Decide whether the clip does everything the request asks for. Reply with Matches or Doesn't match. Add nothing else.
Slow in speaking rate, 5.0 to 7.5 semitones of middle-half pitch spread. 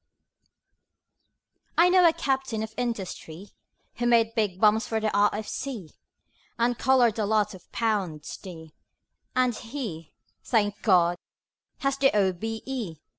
Doesn't match